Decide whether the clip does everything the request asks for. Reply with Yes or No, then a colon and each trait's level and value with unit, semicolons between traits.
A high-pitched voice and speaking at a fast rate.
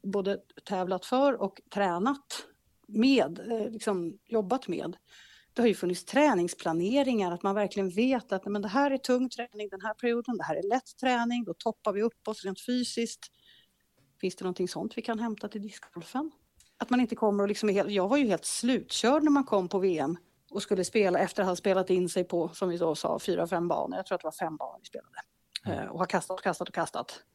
Yes: high, 210 Hz; fast, 210 wpm